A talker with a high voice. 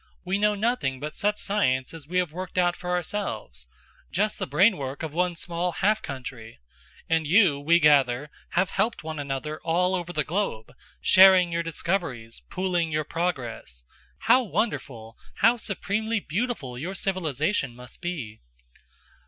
No: medium, 170 Hz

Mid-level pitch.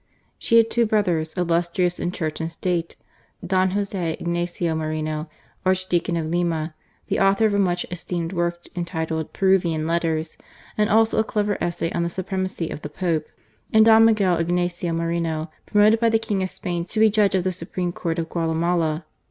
Yes: medium, 175 Hz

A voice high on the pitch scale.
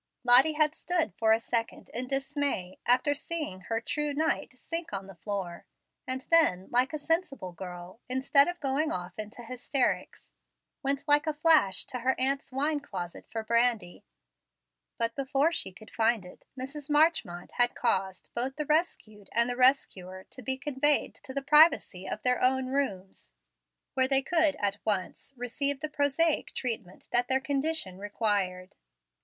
Yes: very high, 255 Hz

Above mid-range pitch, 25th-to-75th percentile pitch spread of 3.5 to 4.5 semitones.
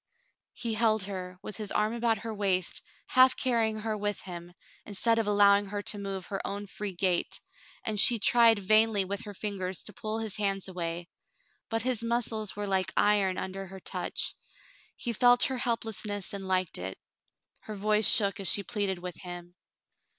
No: high, 205 Hz; narrow, 2.6 semitones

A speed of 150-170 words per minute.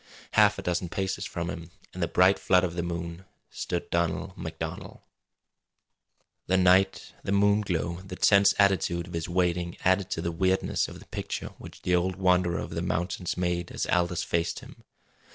No: average, 180 wpm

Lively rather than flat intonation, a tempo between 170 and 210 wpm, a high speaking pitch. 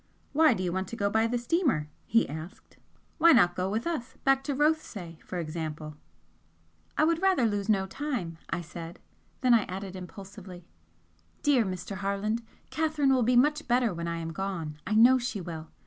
Yes: wide, 6.6 semitones; average, 185 wpm; high, 205 Hz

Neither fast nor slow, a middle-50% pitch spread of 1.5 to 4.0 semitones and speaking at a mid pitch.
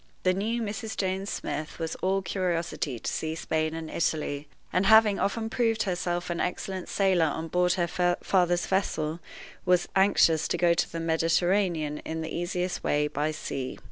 Yes: average, 170 wpm; average, 2.9 semitones; medium, 175 Hz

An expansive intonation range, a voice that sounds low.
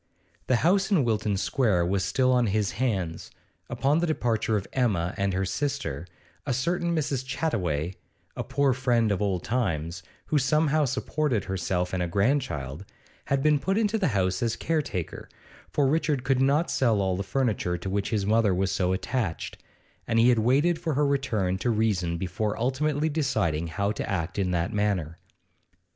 Yes: wide, 6.7 semitones; low, 115 Hz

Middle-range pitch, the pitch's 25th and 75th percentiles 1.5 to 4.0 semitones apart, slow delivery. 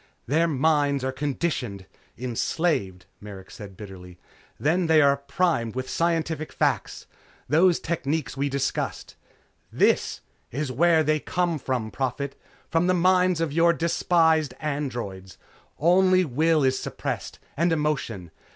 No: medium, 150 Hz; average, 4.6 semitones; slow, 125 wpm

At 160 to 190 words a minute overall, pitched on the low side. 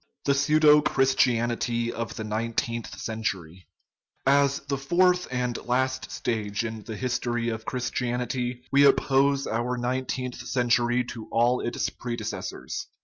No: average, 140 wpm; low, 125 Hz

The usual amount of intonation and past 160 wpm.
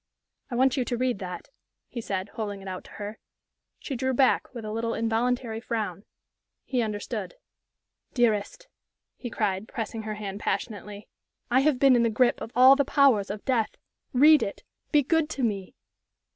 Yes: average, 3.7 semitones; average, 175 wpm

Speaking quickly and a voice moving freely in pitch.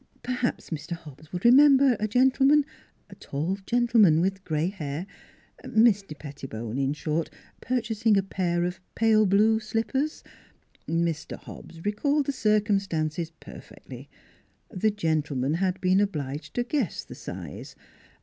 No: average, 140 wpm; wide, 6.2 semitones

